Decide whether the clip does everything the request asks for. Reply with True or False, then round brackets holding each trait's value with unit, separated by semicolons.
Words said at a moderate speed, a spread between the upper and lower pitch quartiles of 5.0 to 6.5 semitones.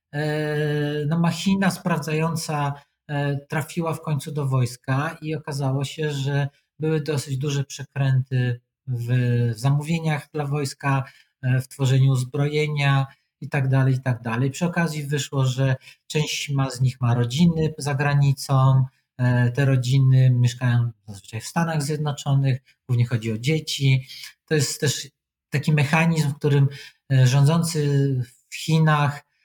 False (120 wpm; 2.5 semitones)